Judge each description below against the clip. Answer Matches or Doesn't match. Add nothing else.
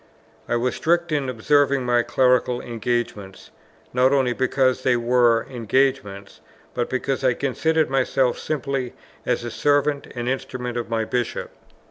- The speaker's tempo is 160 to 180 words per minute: Doesn't match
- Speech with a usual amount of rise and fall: Doesn't match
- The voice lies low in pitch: Matches